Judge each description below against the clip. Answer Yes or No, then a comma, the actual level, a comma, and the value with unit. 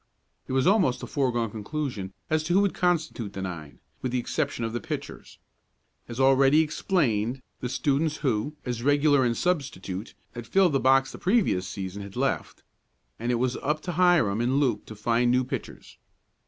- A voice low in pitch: Yes, low, 130 Hz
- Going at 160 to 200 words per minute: Yes, average, 180 wpm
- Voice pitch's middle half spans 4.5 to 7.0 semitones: Yes, average, 5.0 semitones